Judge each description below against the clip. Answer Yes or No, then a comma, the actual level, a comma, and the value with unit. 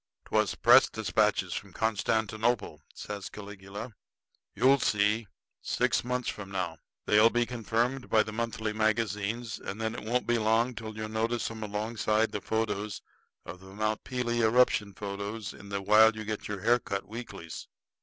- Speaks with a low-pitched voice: Yes, low, 110 Hz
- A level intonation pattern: Yes, narrow, 2.0 semitones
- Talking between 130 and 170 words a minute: Yes, average, 165 wpm